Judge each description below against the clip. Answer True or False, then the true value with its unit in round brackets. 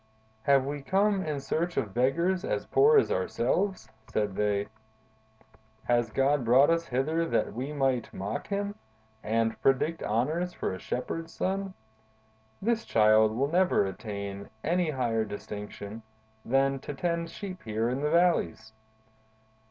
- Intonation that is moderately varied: False (7.4 semitones)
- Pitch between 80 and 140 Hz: True (135 Hz)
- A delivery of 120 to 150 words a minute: True (140 wpm)